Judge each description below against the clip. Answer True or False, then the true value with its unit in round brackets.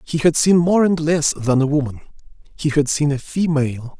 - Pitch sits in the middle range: True (150 Hz)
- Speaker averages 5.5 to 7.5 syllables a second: False (5.1 syllables/s)